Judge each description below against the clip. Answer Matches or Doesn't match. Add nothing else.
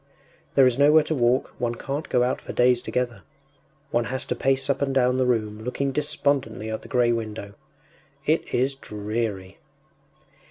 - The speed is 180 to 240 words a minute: Doesn't match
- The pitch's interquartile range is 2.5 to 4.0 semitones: Matches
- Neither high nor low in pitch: Doesn't match